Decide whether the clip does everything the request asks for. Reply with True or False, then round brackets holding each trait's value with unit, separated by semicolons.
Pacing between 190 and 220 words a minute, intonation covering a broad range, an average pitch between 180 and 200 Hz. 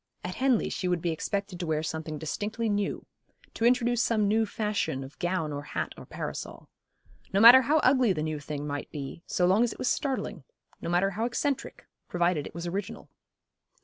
True (195 wpm; 6.3 semitones; 190 Hz)